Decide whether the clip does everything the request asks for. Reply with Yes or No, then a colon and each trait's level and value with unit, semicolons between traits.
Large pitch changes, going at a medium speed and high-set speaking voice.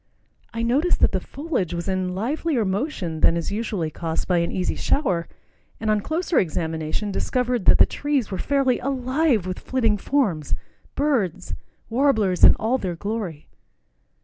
Yes: wide, 6.6 semitones; average, 150 wpm; high, 215 Hz